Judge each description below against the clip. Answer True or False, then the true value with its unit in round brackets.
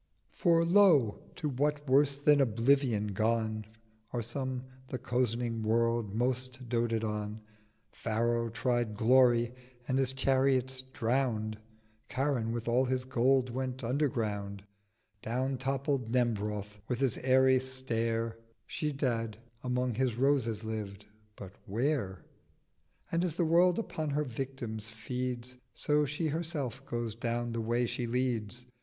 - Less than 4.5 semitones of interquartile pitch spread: True (2.8 semitones)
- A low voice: True (125 Hz)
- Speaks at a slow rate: True (125 wpm)